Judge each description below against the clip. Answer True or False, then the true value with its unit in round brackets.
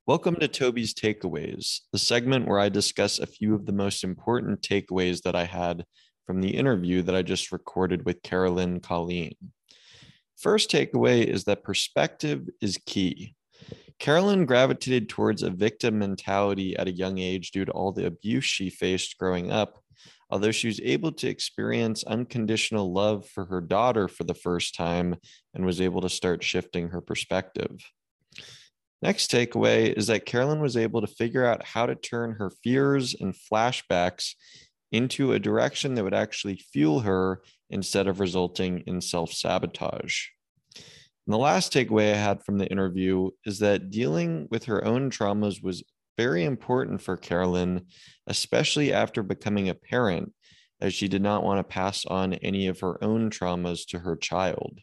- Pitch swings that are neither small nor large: True (3.6 semitones)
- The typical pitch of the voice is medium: False (100 Hz)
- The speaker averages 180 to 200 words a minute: False (165 wpm)